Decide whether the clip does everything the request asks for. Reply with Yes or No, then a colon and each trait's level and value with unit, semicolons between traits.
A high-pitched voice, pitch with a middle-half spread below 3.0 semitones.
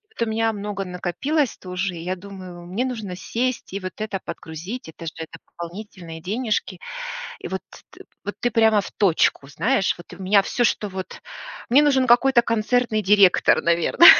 No: high, 200 Hz; average, 4.4 semitones